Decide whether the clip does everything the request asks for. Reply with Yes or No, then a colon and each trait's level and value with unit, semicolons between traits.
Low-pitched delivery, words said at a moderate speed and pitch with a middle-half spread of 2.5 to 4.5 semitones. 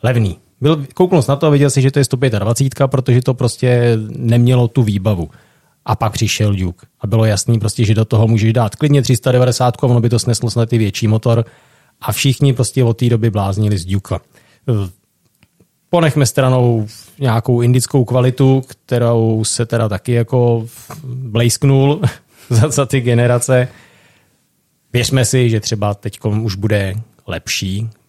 Yes: low, 120 Hz; average, 155 wpm; average, 2.9 semitones